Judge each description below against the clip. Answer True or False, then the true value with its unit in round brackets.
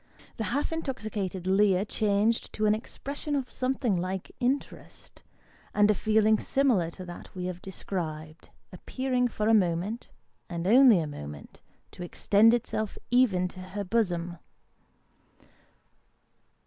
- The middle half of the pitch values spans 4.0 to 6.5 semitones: True (4.6 semitones)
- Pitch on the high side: True (205 Hz)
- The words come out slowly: True (130 wpm)